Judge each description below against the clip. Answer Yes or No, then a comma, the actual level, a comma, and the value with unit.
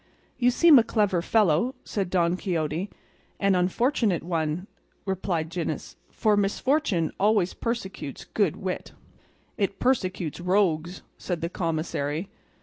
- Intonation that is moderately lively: Yes, average, 3.7 semitones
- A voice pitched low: No, medium, 185 Hz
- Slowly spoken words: Yes, slow, 125 wpm